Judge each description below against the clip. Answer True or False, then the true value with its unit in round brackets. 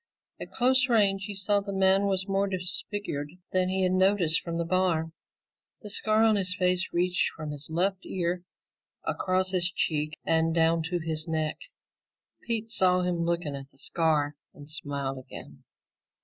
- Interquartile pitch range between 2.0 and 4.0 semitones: True (3.2 semitones)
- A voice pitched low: False (180 Hz)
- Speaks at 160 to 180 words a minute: True (165 wpm)